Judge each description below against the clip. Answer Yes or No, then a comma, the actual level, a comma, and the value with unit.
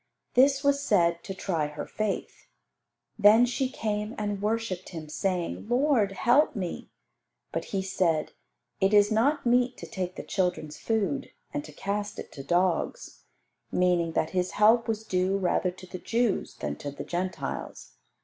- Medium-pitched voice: No, high, 195 Hz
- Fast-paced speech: No, average, 160 wpm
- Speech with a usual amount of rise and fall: Yes, average, 4.1 semitones